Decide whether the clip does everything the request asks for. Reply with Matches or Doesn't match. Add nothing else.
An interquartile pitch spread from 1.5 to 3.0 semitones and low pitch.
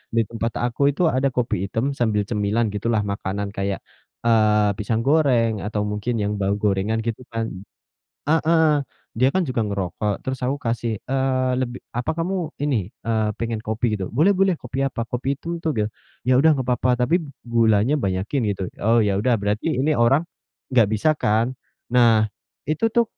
Doesn't match